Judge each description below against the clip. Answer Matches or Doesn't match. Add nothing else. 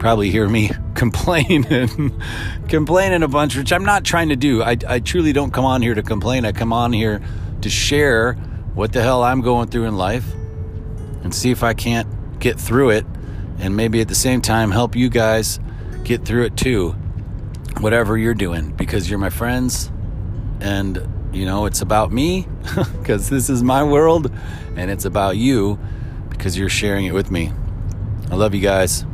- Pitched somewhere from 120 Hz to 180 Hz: Doesn't match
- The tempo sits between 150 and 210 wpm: Matches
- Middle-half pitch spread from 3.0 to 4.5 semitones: Matches